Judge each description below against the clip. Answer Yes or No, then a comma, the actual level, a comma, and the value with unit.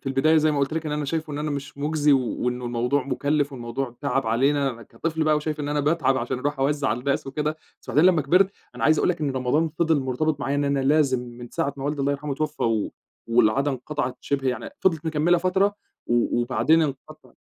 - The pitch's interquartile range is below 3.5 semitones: Yes, average, 2.7 semitones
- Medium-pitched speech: Yes, medium, 145 Hz